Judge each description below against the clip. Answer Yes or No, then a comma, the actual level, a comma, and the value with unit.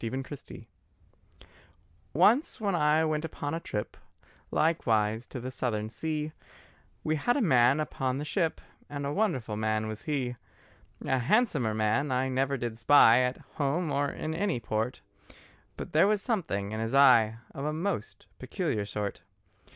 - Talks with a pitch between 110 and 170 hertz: Yes, low, 135 Hz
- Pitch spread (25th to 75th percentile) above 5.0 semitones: Yes, wide, 5.6 semitones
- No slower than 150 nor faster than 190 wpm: Yes, average, 160 wpm